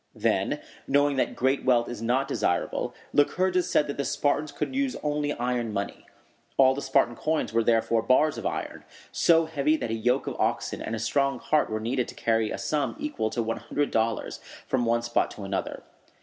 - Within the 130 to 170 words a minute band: No, average, 200 wpm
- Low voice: Yes, low, 130 Hz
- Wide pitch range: No, average, 4.2 semitones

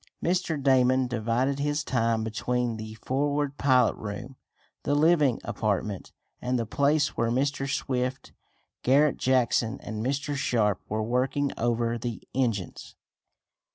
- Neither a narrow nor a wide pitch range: Yes, average, 3.4 semitones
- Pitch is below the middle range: Yes, low, 125 Hz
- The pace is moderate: No, slow, 125 wpm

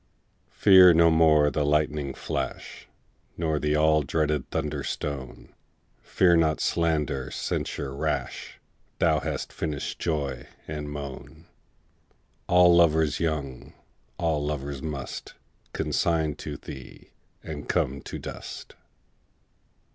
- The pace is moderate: No, slow, 110 wpm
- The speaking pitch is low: Yes, very low, 75 Hz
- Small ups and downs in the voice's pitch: Yes, narrow, 2.1 semitones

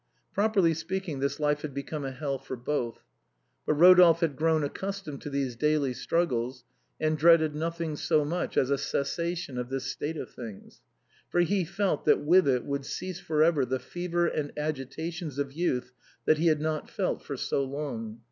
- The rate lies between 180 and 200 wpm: Yes, average, 185 wpm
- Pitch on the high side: No, medium, 150 Hz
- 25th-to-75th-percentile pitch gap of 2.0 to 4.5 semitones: Yes, average, 3.6 semitones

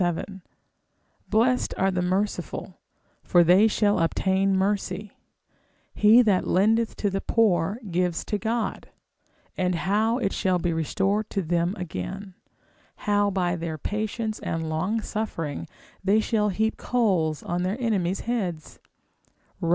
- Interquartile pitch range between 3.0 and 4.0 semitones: Yes, average, 3.5 semitones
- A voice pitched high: Yes, high, 195 Hz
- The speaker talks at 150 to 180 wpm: No, slow, 135 wpm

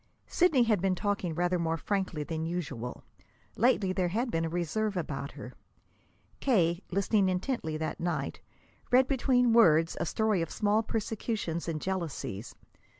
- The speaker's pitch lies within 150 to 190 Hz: Yes, medium, 185 Hz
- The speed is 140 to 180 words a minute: Yes, average, 150 wpm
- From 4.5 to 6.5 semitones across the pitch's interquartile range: Yes, average, 5.0 semitones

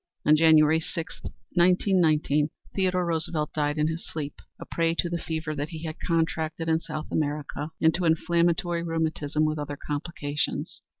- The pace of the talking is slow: No, average, 160 wpm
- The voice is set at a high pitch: No, medium, 160 Hz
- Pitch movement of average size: No, narrow, 1.8 semitones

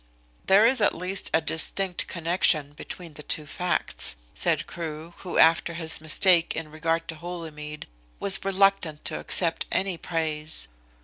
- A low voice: No, medium, 165 Hz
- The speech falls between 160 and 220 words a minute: No, average, 145 wpm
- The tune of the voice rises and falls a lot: No, average, 2.7 semitones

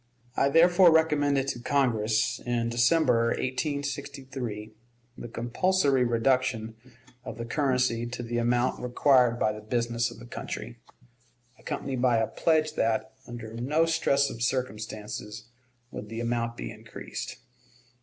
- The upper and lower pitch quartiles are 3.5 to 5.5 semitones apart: No, average, 3.1 semitones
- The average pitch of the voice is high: No, low, 120 Hz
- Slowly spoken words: Yes, slow, 130 wpm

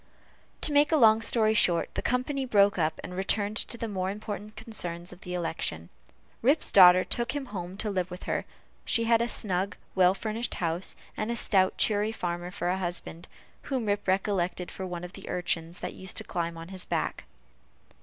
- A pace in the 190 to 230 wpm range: Yes, average, 195 wpm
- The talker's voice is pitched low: No, high, 190 Hz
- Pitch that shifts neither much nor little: Yes, average, 3.7 semitones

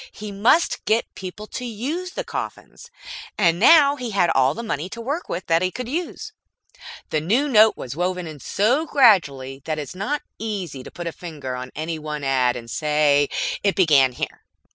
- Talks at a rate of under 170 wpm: No, average, 195 wpm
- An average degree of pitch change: No, wide, 7.7 semitones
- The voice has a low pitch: No, medium, 185 Hz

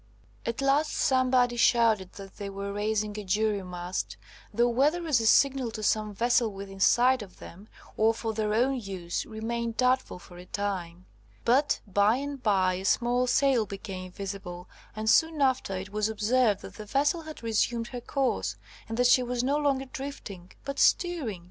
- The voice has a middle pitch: No, high, 225 Hz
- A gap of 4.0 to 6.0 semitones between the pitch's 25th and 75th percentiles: Yes, average, 4.4 semitones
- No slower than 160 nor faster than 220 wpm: Yes, average, 180 wpm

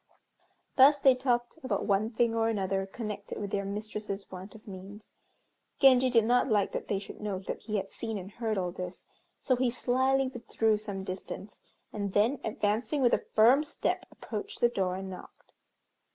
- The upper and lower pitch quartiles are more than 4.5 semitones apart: No, average, 3.7 semitones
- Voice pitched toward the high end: Yes, high, 215 Hz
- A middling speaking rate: Yes, average, 180 wpm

